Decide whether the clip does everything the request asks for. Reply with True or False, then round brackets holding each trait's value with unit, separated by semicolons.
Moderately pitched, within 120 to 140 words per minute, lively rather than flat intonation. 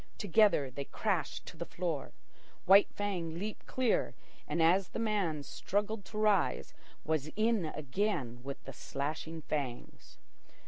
True (170 Hz; 135 wpm; 5.7 semitones)